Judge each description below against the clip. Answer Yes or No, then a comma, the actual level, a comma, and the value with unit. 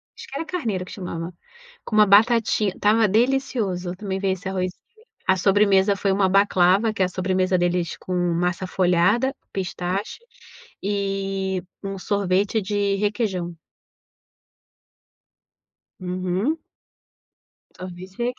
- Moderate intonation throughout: No, narrow, 2.2 semitones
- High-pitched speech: Yes, high, 195 Hz